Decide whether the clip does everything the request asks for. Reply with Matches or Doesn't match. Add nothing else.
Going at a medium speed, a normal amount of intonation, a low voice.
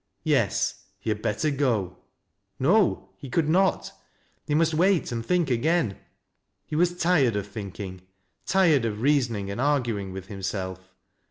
Doesn't match